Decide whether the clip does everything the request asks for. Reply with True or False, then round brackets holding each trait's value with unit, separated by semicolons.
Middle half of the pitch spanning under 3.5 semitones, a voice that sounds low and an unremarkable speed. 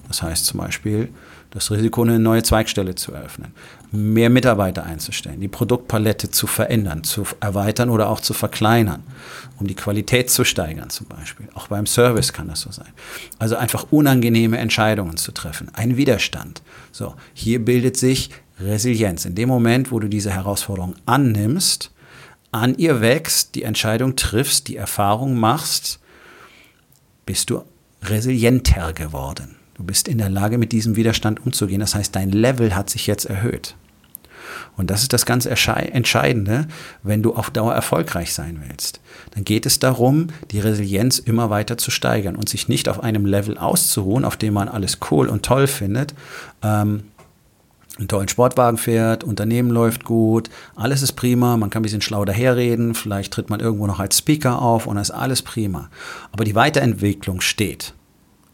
True (3.1 semitones; 110 Hz; 165 wpm)